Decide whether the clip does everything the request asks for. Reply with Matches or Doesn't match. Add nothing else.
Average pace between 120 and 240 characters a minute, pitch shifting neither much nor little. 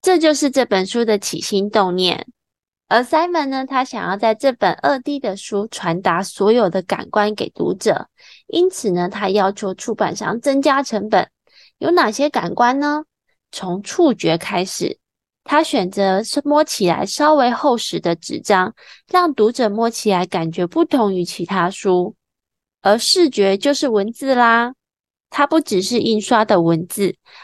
Doesn't match